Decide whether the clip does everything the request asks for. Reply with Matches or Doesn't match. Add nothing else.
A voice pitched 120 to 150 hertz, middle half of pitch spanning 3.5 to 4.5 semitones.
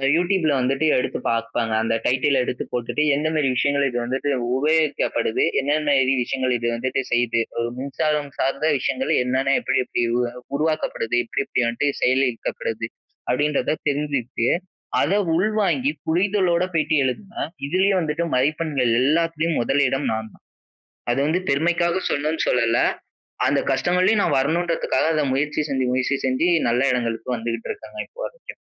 Matches